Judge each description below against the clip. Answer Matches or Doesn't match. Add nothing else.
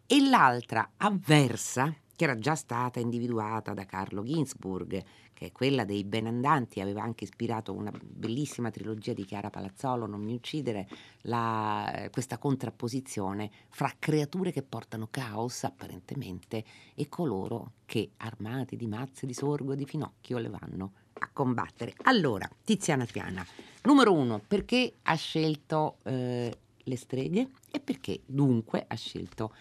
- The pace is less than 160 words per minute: Matches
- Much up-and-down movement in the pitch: Doesn't match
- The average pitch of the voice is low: Matches